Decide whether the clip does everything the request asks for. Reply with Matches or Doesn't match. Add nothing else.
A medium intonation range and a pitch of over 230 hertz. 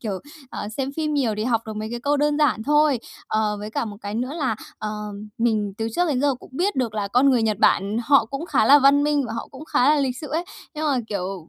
Matches